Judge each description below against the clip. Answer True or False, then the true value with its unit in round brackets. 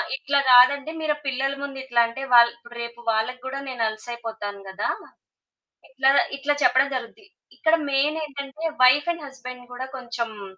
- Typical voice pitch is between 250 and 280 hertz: True (260 Hz)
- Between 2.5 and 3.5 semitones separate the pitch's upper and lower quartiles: True (3.0 semitones)